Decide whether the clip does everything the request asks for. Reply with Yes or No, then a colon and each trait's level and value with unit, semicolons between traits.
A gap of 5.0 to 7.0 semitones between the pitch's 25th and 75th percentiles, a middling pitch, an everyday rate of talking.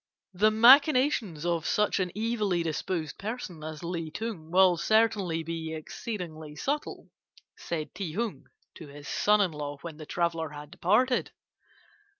Yes: average, 5.3 semitones; medium, 175 Hz; average, 145 wpm